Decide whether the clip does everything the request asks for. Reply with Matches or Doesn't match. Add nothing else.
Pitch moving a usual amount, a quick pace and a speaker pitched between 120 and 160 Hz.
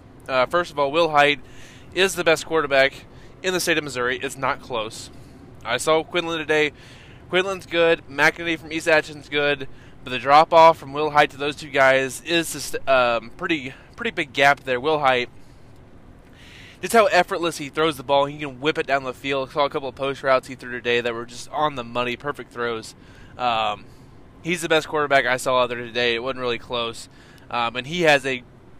Matches